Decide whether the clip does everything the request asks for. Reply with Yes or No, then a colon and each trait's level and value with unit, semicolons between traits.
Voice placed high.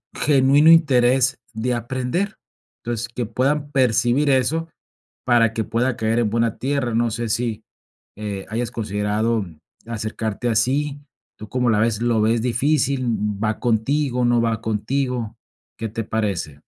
No: low, 120 Hz